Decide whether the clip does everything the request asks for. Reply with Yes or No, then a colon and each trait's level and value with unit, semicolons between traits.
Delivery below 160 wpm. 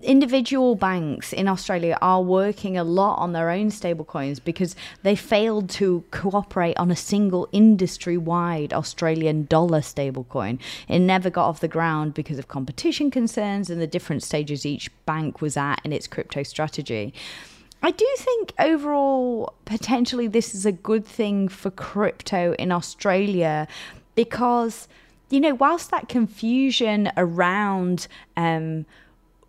Yes: average, 140 wpm